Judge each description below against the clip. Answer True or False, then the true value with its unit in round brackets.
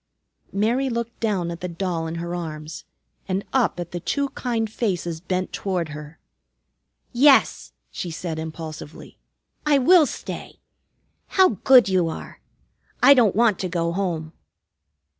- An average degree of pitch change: False (5.9 semitones)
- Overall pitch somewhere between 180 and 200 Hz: True (185 Hz)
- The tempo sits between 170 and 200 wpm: False (140 wpm)